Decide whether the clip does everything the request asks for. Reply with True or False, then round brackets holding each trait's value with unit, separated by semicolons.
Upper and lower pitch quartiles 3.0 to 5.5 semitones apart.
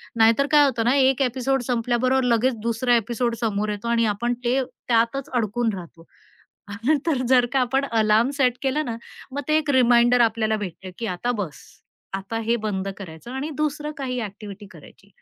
True (3.3 semitones)